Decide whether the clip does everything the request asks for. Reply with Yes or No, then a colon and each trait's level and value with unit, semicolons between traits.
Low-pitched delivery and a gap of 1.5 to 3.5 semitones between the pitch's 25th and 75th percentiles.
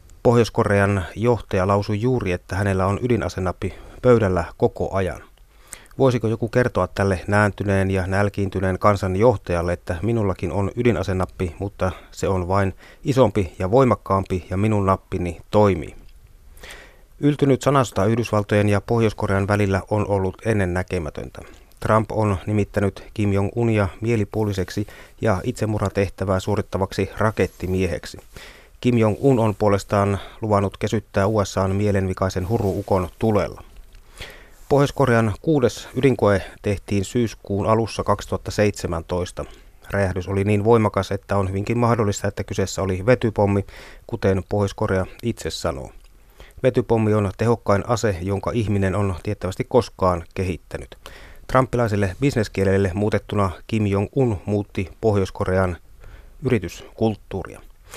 Yes: low, 100 Hz; average, 2.7 semitones